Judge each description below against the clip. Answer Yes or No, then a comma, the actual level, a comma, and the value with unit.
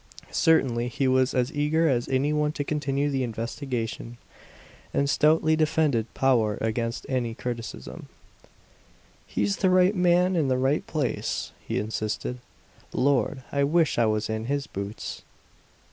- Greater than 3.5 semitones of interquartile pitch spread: Yes, average, 4.3 semitones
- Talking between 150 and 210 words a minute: No, average, 140 wpm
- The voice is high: No, low, 130 Hz